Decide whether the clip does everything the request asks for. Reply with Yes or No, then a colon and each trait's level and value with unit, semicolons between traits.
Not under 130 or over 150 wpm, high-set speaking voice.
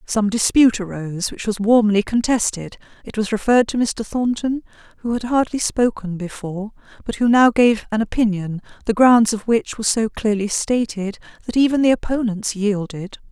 No: average, 165 wpm; high, 220 Hz